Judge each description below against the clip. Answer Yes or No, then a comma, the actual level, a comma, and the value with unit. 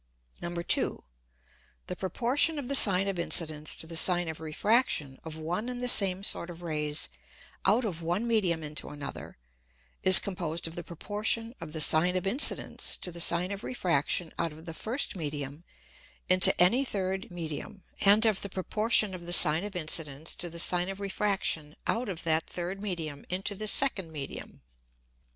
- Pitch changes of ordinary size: Yes, average, 3.9 semitones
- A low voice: No, medium, 180 Hz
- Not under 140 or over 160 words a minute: No, average, 175 wpm